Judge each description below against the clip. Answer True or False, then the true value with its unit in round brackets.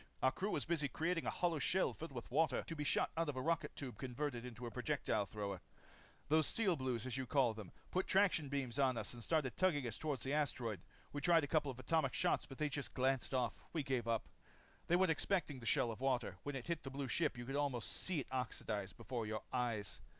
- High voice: False (135 Hz)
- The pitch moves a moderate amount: True (4.4 semitones)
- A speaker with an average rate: False (240 wpm)